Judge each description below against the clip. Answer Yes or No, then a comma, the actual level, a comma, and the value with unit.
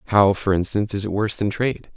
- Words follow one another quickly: Yes, fast, 245 wpm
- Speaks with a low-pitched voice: Yes, low, 105 Hz